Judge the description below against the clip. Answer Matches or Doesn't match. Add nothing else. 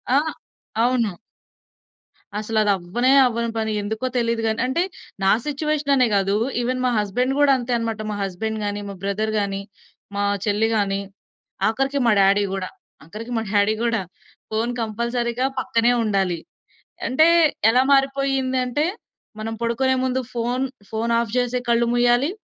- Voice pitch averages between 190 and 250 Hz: Matches